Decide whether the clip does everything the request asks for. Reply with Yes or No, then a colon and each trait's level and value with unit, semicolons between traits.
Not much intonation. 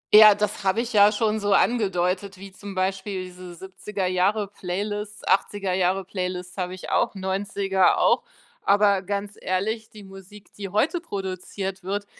Yes: narrow, 1.8 semitones